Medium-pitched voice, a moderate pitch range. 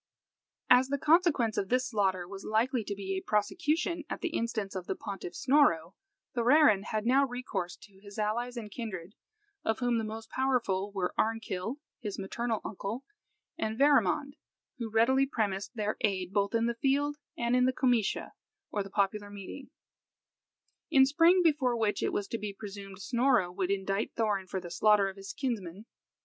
No: high, 220 Hz; average, 4.4 semitones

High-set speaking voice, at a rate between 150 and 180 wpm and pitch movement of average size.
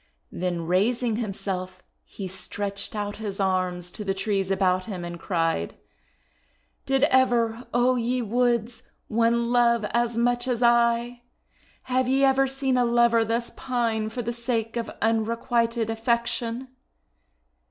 No: high, 230 Hz; average, 140 wpm; average, 3.3 semitones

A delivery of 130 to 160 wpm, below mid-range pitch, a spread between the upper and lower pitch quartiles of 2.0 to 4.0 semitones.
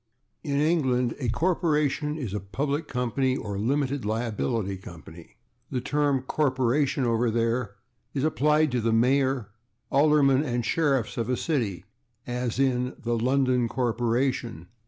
Yes: slow, 135 wpm; low, 125 Hz; average, 3.5 semitones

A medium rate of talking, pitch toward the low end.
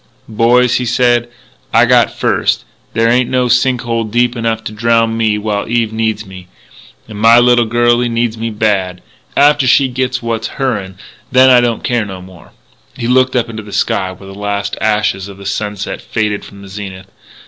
Yes: average, 185 wpm; low, 115 Hz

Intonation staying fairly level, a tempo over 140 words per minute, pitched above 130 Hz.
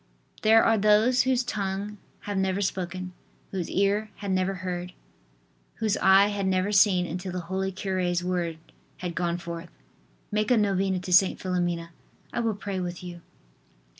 Yes: narrow, 2.3 semitones; average, 160 wpm; high, 190 Hz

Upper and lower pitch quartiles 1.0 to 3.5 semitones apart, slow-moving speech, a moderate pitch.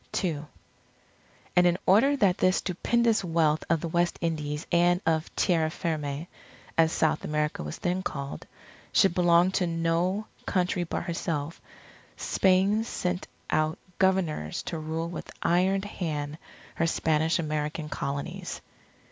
Yes: average, 2.8 semitones; slow, 130 wpm; medium, 170 Hz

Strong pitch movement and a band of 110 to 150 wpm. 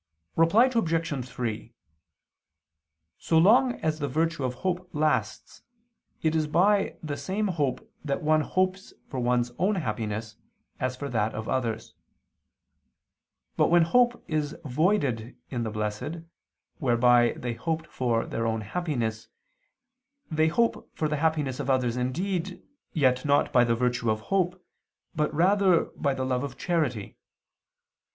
Yes: wide, 5.7 semitones; average, 140 wpm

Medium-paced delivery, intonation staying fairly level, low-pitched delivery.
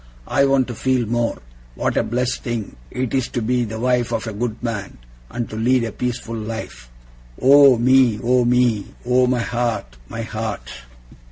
Yes: average, 180 wpm; narrow, 2.1 semitones; low, 120 Hz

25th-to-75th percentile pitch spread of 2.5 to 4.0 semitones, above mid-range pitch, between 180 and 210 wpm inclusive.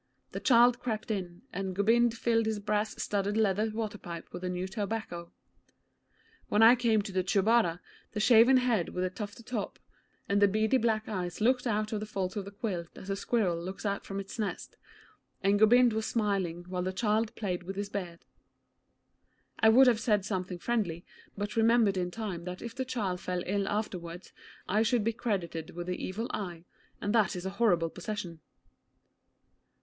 Yes: average, 3.4 semitones; high, 205 Hz; average, 185 wpm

